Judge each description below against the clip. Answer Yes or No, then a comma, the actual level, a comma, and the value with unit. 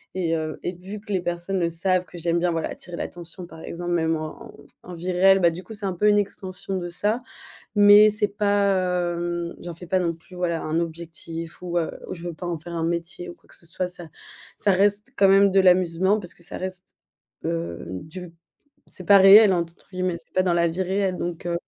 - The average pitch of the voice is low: No, medium, 175 Hz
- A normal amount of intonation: No, narrow, 2.1 semitones